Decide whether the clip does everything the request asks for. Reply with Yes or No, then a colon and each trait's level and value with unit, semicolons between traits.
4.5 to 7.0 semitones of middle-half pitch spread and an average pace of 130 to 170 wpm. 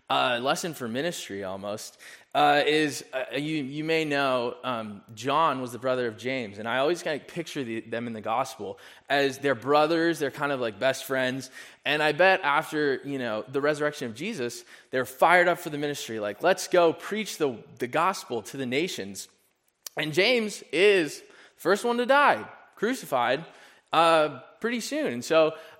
No: average, 4.8 semitones; average, 185 wpm